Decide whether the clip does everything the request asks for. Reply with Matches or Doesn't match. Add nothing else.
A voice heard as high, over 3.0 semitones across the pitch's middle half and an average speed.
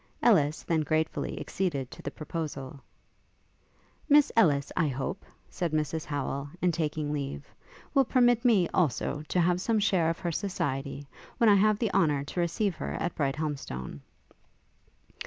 Doesn't match